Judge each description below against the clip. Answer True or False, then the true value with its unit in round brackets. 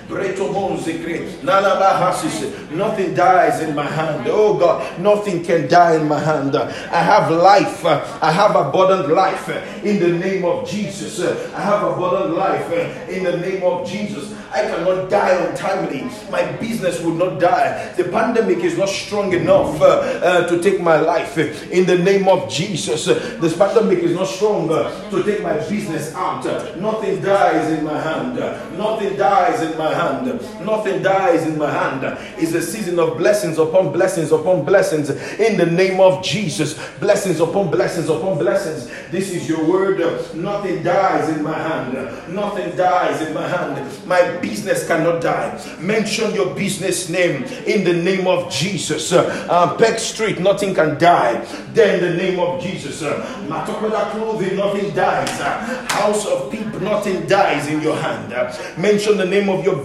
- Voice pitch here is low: False (185 Hz)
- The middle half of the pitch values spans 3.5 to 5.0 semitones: False (3.1 semitones)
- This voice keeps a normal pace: True (165 wpm)